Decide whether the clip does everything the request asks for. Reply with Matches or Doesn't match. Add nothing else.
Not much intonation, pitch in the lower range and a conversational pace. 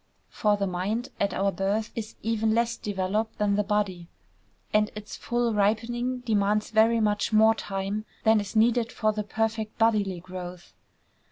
Doesn't match